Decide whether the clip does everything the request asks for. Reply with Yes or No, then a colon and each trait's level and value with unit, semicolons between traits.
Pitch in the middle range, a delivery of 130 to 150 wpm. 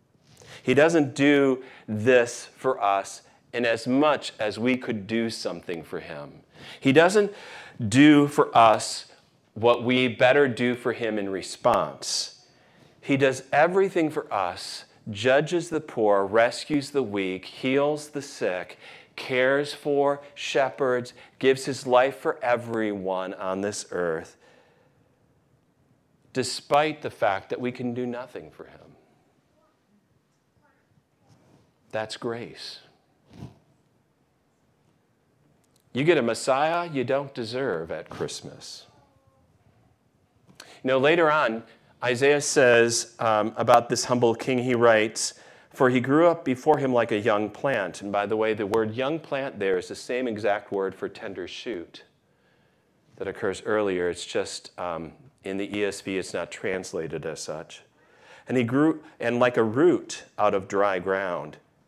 No: low, 125 Hz; slow, 135 wpm